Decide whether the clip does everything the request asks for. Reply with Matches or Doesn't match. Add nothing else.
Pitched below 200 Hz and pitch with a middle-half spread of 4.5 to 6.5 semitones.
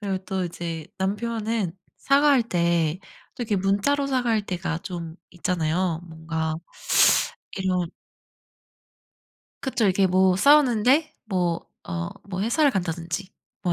Matches